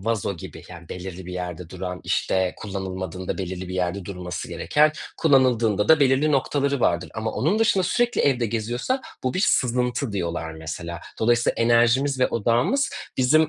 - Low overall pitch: Yes, low, 115 Hz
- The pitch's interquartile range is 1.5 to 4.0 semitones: No, wide, 6.7 semitones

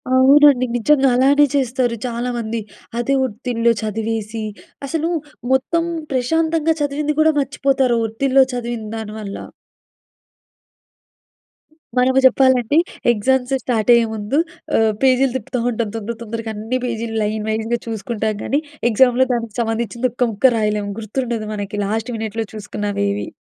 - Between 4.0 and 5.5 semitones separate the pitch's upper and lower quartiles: No, average, 3.1 semitones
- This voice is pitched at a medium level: No, high, 235 Hz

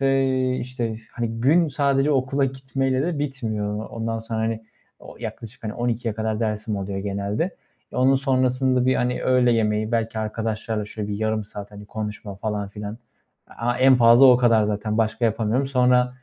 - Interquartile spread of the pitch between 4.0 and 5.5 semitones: No, average, 3.2 semitones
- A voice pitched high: No, low, 115 Hz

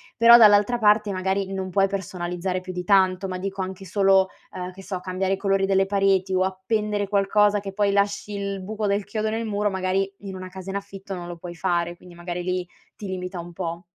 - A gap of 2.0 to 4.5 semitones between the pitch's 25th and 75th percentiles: No, narrow, 1.5 semitones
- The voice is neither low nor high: No, high, 195 Hz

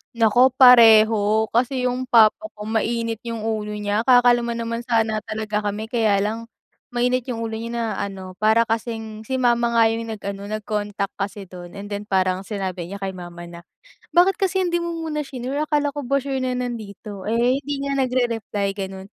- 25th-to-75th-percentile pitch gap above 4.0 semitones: No, average, 3.3 semitones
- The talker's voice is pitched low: No, high, 225 Hz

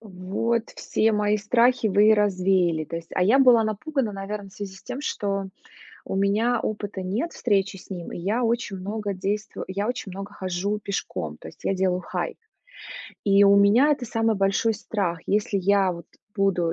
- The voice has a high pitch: Yes, high, 200 Hz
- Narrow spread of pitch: Yes, narrow, 2.3 semitones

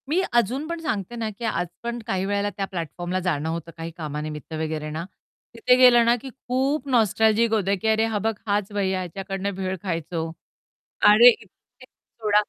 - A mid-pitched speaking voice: No, high, 205 Hz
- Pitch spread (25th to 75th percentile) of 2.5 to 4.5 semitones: No, average, 4.9 semitones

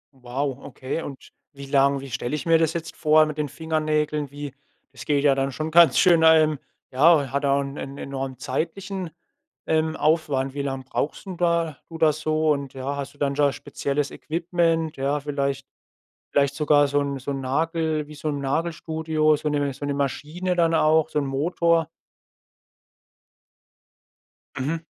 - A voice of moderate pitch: Yes, medium, 150 Hz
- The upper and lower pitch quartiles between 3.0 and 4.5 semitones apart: No, narrow, 2.5 semitones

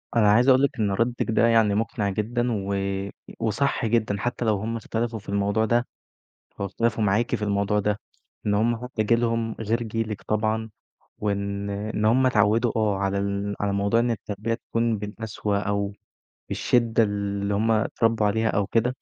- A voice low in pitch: Yes, low, 110 Hz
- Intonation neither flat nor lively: No, narrow, 2.2 semitones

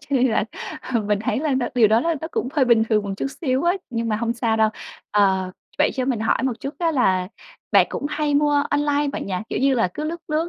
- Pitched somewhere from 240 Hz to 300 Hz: Yes, very high, 255 Hz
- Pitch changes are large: No, average, 4.9 semitones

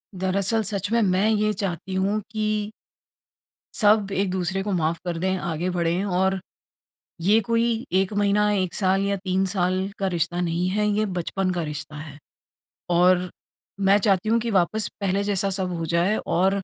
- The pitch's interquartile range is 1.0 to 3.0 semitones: Yes, narrow, 2.4 semitones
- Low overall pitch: No, high, 190 Hz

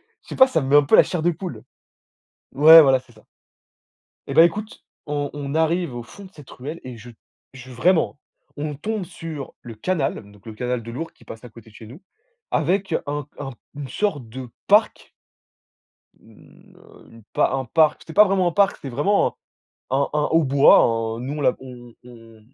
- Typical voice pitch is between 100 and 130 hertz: No, medium, 140 Hz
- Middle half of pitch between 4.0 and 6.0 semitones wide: Yes, average, 4.9 semitones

